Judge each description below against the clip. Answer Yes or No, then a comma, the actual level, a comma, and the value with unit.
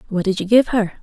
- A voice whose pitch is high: Yes, high, 205 Hz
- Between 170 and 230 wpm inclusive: No, fast, 290 wpm